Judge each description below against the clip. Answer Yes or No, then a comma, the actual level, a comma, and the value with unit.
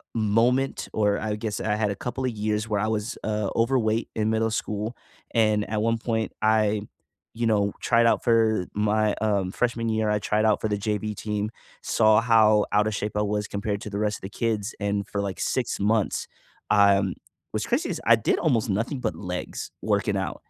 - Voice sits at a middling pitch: No, low, 110 Hz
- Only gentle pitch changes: Yes, narrow, 1.5 semitones